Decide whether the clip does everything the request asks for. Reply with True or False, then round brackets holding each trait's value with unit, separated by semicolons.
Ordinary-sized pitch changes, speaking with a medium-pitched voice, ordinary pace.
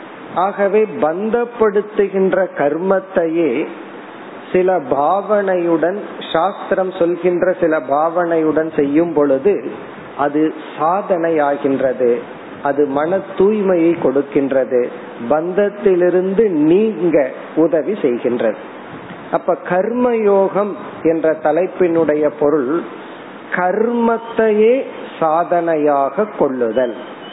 False (4.8 semitones; 180 Hz; 60 wpm)